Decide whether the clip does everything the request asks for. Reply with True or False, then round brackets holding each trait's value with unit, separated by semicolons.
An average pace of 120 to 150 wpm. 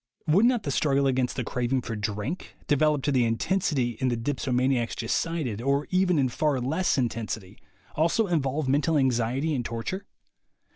False (165 wpm)